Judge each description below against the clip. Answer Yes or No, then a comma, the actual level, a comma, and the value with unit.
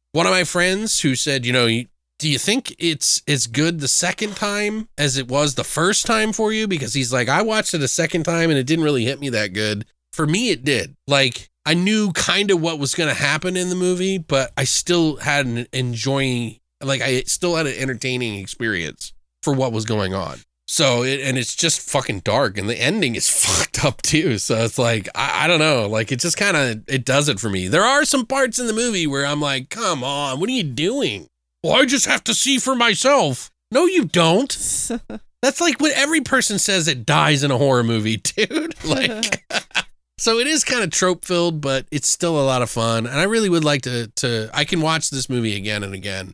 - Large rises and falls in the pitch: Yes, wide, 7.4 semitones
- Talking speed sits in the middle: No, fast, 230 wpm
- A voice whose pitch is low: No, medium, 145 Hz